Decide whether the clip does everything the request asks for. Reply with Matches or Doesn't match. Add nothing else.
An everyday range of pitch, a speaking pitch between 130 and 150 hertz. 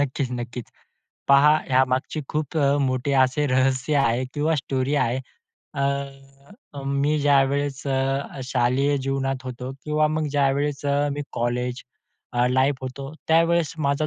Doesn't match